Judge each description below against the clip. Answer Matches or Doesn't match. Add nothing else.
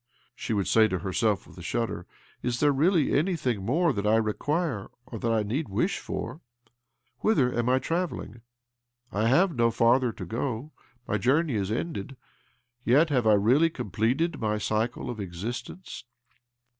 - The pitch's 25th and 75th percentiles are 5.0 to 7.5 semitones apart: Matches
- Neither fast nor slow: Matches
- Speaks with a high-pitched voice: Doesn't match